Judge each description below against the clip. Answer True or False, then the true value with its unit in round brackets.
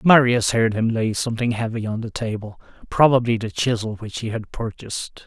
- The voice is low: True (115 Hz)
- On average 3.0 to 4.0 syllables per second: False (5.4 syllables/s)